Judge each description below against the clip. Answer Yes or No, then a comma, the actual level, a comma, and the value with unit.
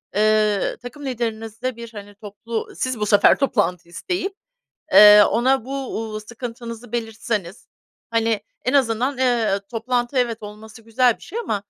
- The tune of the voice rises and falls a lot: No, average, 2.8 semitones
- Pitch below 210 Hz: No, high, 230 Hz